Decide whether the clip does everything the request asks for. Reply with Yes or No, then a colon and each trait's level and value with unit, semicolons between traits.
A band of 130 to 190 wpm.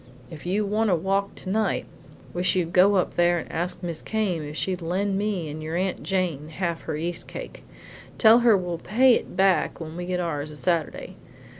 No: fast, 205 wpm